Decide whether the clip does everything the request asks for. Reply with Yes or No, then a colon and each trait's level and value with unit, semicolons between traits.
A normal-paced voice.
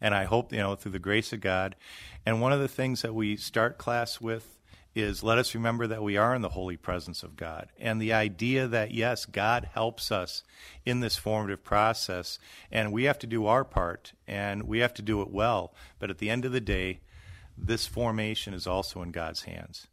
No: fast, 220 wpm